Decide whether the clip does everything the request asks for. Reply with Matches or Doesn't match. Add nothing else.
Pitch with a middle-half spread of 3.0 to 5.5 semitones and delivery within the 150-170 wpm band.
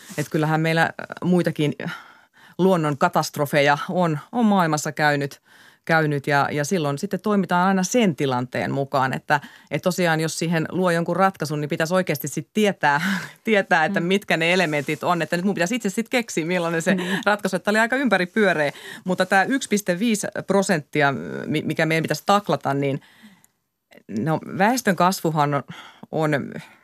Matches